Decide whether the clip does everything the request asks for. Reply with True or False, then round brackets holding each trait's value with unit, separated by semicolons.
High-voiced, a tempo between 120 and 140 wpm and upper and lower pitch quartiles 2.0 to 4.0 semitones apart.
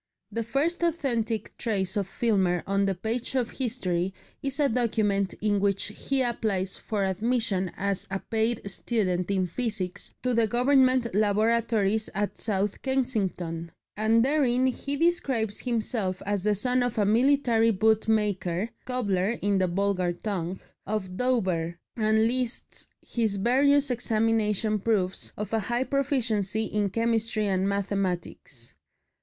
True (215 Hz; 135 wpm; 3.6 semitones)